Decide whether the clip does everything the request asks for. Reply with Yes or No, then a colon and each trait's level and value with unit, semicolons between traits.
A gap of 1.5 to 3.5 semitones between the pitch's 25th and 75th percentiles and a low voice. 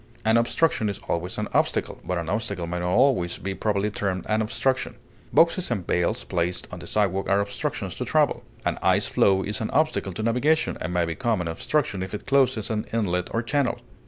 No: average, 4.6 semitones; low, 105 Hz